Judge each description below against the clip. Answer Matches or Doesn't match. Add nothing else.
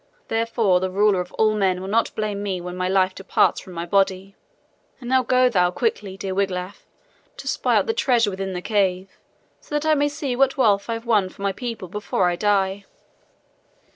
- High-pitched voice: Matches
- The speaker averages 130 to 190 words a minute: Doesn't match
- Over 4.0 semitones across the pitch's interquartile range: Doesn't match